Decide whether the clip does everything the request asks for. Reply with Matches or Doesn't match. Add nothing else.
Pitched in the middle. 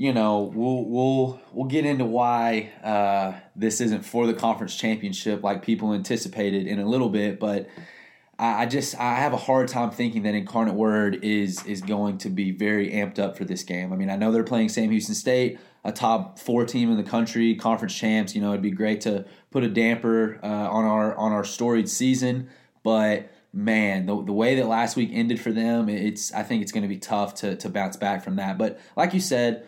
Doesn't match